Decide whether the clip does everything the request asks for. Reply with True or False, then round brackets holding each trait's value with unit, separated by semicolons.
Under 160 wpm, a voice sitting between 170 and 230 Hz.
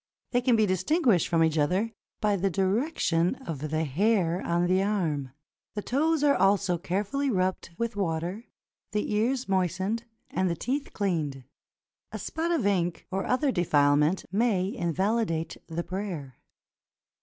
True (145 wpm; 190 Hz)